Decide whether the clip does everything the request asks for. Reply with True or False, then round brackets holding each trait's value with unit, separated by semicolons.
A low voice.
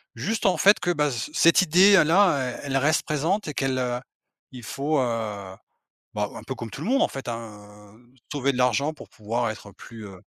True (130 Hz)